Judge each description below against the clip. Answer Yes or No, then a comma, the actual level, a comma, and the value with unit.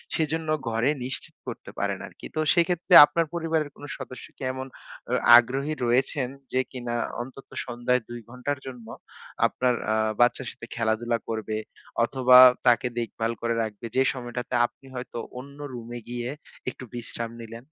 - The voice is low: Yes, low, 125 Hz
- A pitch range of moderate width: No, narrow, 2.1 semitones